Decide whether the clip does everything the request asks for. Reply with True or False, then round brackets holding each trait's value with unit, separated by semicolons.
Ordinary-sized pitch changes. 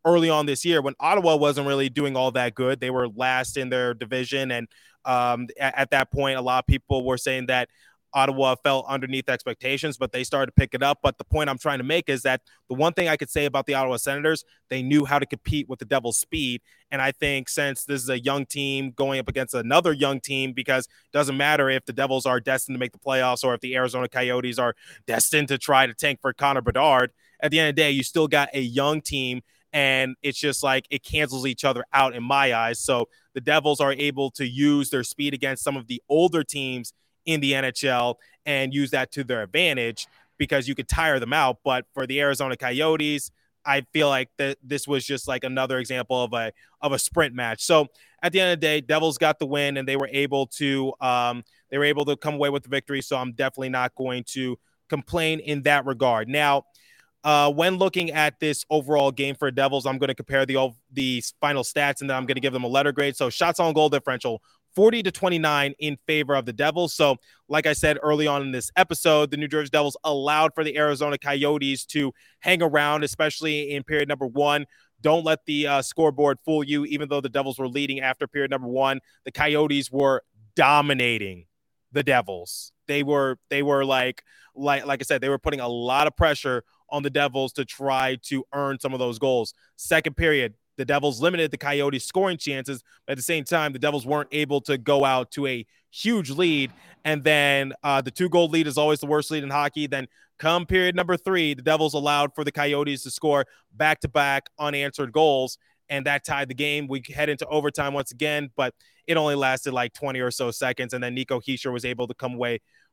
False (2.2 semitones)